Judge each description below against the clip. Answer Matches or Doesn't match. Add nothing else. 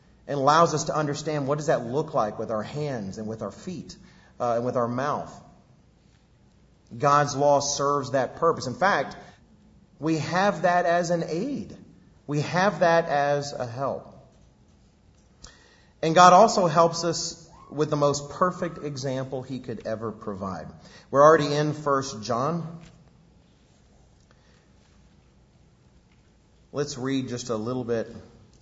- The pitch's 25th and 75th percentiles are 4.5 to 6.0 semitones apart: Matches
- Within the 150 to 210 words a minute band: Doesn't match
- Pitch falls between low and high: Matches